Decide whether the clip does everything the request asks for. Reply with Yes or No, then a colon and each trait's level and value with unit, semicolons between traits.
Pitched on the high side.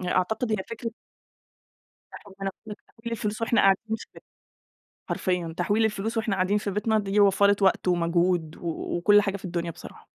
Yes: high, 200 Hz